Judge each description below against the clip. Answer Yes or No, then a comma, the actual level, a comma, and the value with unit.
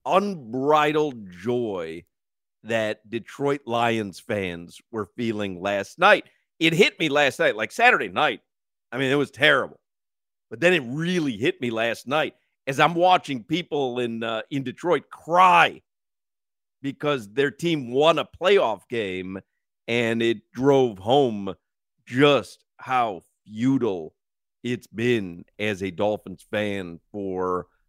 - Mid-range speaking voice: No, low, 120 Hz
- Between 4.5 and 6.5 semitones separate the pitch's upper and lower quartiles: Yes, wide, 5.6 semitones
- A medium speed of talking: No, slow, 130 wpm